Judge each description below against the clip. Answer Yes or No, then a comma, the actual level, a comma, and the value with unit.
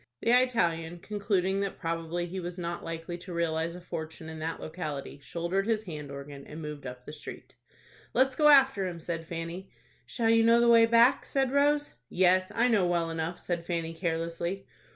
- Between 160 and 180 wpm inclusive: No, average, 190 wpm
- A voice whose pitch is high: No, medium, 175 Hz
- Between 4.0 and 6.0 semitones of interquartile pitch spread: Yes, average, 4.5 semitones